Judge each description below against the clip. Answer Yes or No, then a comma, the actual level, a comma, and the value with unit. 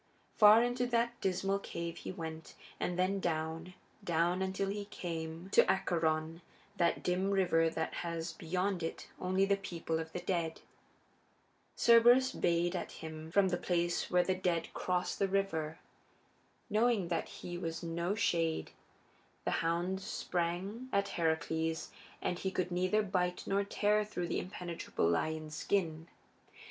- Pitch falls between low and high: Yes, medium, 180 Hz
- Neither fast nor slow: Yes, average, 145 wpm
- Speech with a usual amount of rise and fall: Yes, average, 3.1 semitones